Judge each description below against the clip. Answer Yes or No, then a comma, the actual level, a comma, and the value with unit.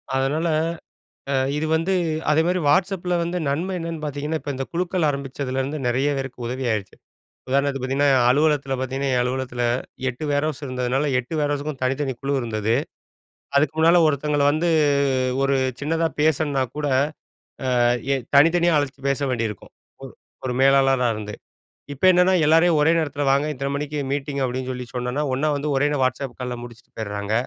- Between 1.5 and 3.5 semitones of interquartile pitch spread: Yes, average, 2.9 semitones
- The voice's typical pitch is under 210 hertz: Yes, medium, 140 Hz